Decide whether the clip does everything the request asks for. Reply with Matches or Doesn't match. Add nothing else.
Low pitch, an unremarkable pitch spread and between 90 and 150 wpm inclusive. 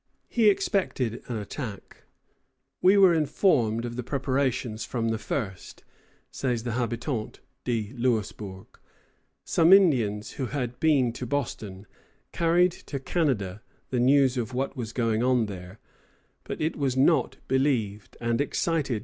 Matches